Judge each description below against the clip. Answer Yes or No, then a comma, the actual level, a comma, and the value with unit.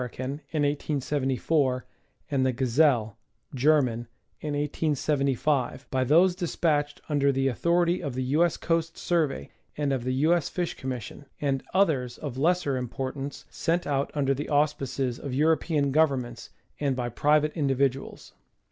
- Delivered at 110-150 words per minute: Yes, average, 140 wpm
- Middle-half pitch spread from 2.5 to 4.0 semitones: Yes, average, 2.9 semitones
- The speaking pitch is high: No, medium, 140 Hz